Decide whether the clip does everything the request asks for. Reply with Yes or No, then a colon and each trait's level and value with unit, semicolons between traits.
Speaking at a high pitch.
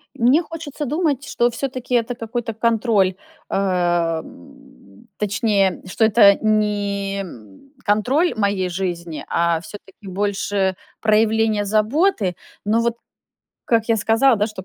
Yes: high, 215 Hz